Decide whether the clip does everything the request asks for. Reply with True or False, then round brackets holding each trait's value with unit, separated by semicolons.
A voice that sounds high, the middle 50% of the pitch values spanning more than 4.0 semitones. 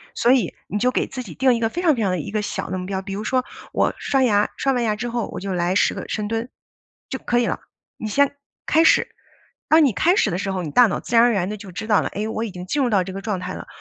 True (220 Hz; 4.4 semitones)